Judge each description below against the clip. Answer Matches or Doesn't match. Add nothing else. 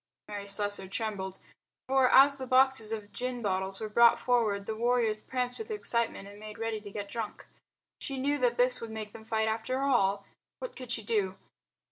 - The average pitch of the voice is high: Matches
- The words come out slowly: Doesn't match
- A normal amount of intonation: Matches